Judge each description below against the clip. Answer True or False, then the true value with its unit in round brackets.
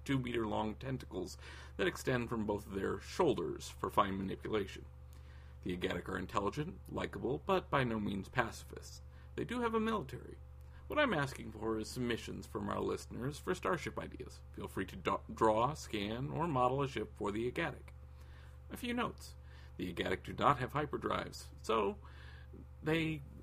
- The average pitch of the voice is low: True (95 Hz)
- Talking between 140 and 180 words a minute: True (165 wpm)